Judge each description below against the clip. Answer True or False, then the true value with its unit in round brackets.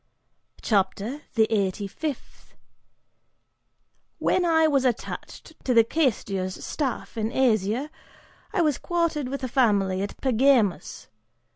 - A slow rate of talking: True (115 wpm)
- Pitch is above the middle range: True (250 Hz)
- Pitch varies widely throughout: True (5.9 semitones)